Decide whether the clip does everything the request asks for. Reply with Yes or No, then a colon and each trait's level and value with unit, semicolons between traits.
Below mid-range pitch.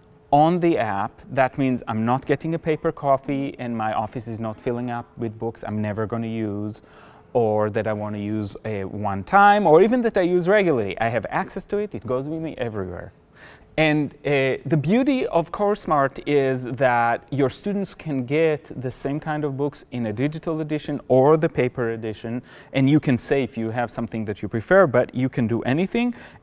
Yes: low, 130 Hz